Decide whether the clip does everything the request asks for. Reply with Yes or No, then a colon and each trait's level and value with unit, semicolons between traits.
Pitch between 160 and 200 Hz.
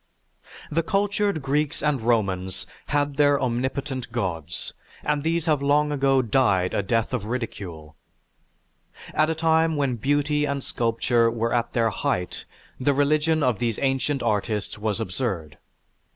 No: low, 130 Hz